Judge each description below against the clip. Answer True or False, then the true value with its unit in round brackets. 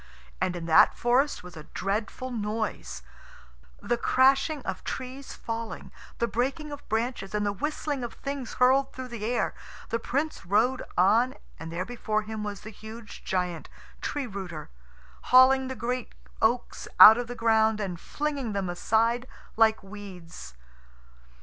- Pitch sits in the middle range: False (225 Hz)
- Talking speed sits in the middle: True (150 wpm)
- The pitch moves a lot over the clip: False (4.3 semitones)